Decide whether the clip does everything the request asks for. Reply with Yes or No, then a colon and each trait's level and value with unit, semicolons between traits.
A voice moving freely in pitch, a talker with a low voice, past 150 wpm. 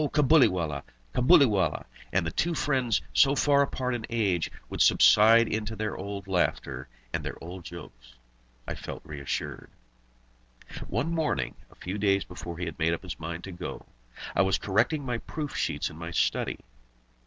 Yes: wide, 6.7 semitones; low, 100 Hz; average, 165 wpm